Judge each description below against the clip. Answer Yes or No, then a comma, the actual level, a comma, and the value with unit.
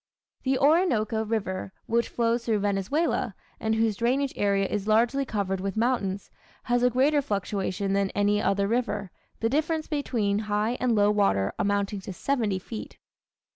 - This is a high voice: Yes, high, 215 Hz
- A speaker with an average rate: Yes, average, 155 wpm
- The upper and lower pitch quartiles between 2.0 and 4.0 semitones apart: Yes, average, 3.6 semitones